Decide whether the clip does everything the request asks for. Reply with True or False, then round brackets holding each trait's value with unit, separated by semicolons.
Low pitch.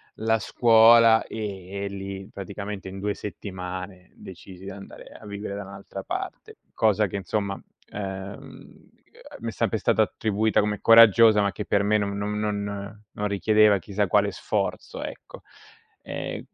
True (100 Hz)